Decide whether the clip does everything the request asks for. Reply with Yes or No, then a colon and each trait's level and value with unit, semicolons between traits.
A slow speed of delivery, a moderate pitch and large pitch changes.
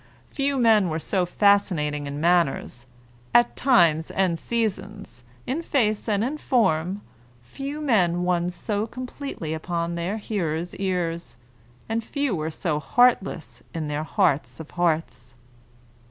Yes: slow, 130 wpm; medium, 180 Hz; wide, 5.7 semitones